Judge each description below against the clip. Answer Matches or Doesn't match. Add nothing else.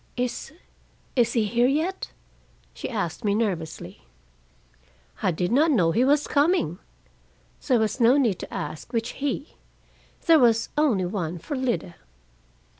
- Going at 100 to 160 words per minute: Matches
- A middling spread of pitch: Doesn't match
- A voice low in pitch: Doesn't match